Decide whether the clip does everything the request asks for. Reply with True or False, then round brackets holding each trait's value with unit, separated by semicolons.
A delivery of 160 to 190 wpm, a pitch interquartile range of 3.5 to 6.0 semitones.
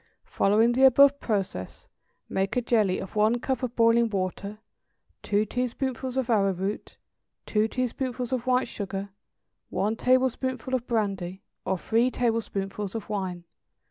False (140 wpm; 4.1 semitones)